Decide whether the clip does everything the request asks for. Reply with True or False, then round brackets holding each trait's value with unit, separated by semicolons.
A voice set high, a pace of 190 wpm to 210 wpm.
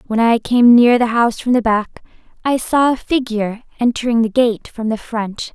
True (235 Hz; 205 wpm)